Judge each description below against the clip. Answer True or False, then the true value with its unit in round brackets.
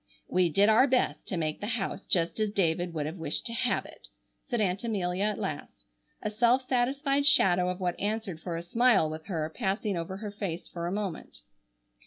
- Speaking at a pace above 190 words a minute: True (205 wpm)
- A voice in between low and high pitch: False (195 Hz)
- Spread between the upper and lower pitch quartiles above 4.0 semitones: True (4.4 semitones)